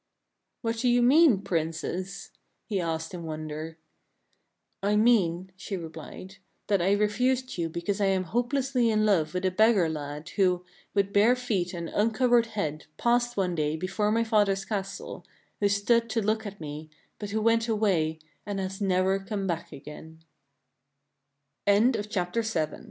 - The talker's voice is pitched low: No, high, 200 Hz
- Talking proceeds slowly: No, average, 145 wpm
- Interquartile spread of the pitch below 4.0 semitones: No, average, 4.9 semitones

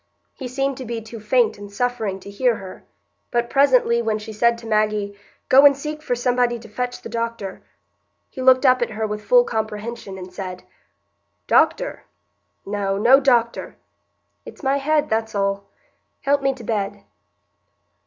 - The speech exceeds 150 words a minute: Yes, average, 165 wpm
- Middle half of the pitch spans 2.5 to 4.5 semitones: Yes, average, 3.5 semitones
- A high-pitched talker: Yes, high, 235 Hz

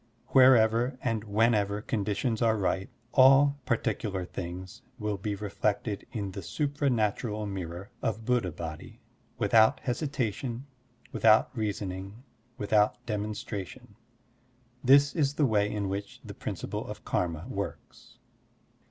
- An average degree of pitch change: Yes, average, 3.5 semitones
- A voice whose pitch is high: No, low, 110 Hz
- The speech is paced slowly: Yes, slow, 115 wpm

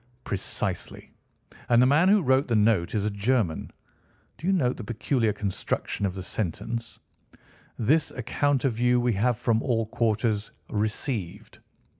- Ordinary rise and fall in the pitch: Yes, average, 3.4 semitones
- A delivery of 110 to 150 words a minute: Yes, average, 145 wpm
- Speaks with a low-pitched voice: Yes, low, 115 Hz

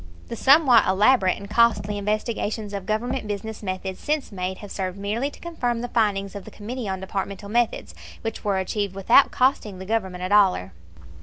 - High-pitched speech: Yes, high, 210 Hz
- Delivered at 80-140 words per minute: No, average, 180 wpm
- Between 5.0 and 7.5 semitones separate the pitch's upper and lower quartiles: No, average, 3.3 semitones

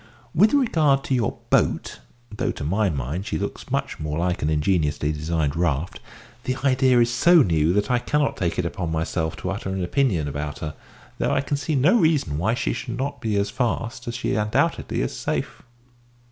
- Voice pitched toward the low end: Yes, low, 100 Hz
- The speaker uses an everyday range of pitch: No, wide, 8.5 semitones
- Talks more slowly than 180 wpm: No, average, 200 wpm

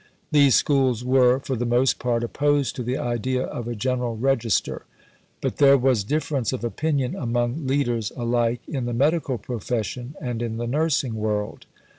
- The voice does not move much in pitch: Yes, narrow, 2.3 semitones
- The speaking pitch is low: Yes, low, 125 Hz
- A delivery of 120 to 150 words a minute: No, average, 165 wpm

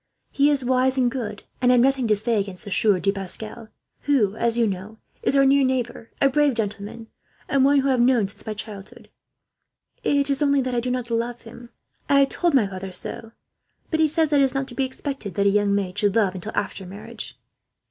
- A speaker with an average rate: No, fast, 235 wpm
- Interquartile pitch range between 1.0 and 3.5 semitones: No, average, 4.6 semitones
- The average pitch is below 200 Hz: No, high, 235 Hz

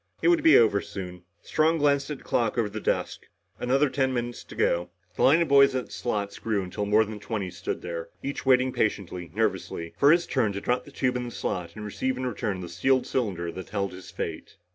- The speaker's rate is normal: No, fast, 230 wpm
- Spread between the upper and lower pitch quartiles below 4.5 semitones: No, wide, 5.5 semitones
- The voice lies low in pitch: Yes, low, 110 Hz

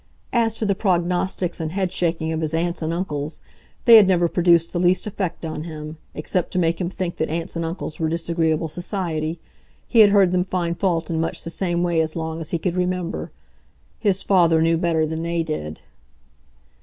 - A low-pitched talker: No, medium, 170 Hz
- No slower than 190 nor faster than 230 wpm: Yes, average, 200 wpm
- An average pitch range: No, narrow, 2.1 semitones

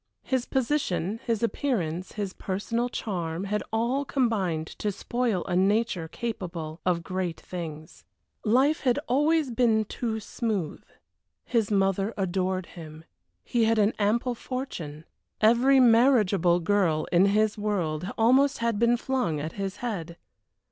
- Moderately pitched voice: No, high, 210 Hz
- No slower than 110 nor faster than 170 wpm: Yes, slow, 135 wpm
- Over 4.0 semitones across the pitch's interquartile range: Yes, average, 5.0 semitones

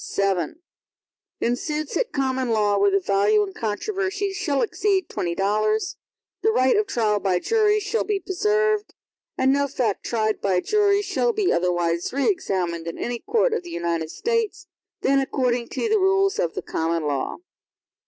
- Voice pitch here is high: Yes, very high, 260 Hz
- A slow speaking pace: No, average, 175 wpm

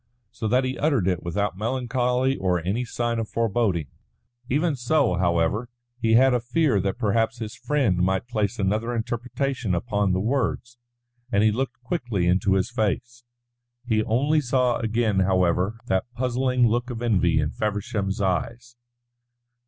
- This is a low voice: Yes, low, 115 Hz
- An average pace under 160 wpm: Yes, average, 150 wpm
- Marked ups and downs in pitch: No, average, 4.1 semitones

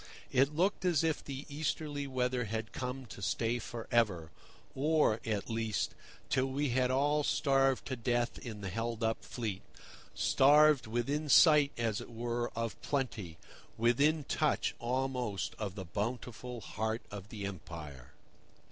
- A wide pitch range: No, average, 3.9 semitones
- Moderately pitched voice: No, low, 120 Hz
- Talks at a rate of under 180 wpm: Yes, average, 145 wpm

